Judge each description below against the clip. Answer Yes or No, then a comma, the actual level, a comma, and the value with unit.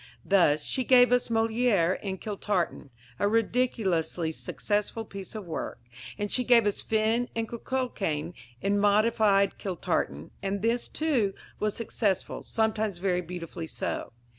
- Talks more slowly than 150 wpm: Yes, slow, 135 wpm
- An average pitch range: Yes, average, 3.5 semitones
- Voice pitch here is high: Yes, high, 205 Hz